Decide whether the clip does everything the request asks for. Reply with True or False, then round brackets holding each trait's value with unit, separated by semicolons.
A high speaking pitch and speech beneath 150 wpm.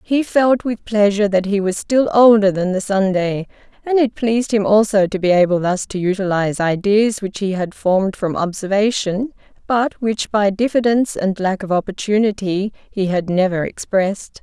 False (205 Hz; 175 wpm)